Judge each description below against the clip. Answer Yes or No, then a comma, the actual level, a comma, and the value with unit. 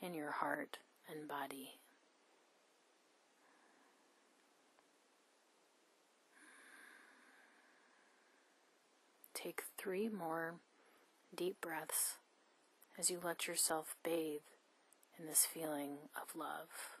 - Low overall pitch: No, medium, 165 Hz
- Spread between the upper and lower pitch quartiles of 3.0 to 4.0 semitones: Yes, average, 3.3 semitones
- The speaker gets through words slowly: Yes, slow, 70 wpm